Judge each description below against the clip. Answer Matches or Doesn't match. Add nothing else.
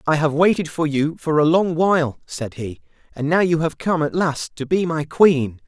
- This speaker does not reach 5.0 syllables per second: Matches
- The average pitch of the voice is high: Doesn't match